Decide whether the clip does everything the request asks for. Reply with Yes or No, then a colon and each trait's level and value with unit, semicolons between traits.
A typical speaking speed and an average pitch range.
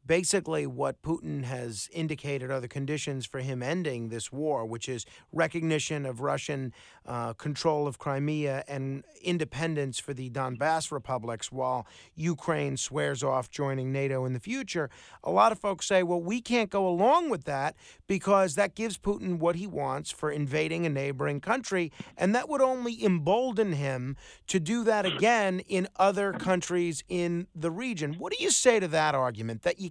No: average, 175 wpm; wide, 5.7 semitones